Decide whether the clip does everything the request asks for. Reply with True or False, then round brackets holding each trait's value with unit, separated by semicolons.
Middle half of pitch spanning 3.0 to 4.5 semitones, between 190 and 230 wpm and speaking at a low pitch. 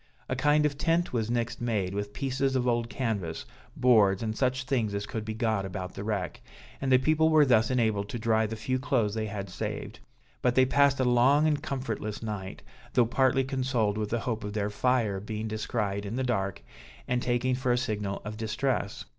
True (3.6 semitones; 205 wpm; 115 Hz)